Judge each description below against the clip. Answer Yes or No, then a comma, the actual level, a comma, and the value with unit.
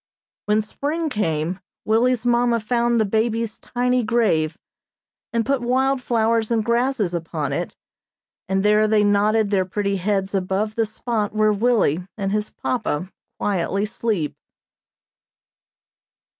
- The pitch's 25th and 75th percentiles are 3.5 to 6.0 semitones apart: No, average, 3.1 semitones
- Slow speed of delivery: Yes, slow, 130 wpm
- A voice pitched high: Yes, high, 215 Hz